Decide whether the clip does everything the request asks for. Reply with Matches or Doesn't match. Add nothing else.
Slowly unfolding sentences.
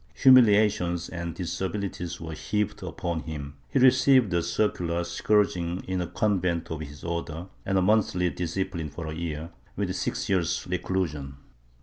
Doesn't match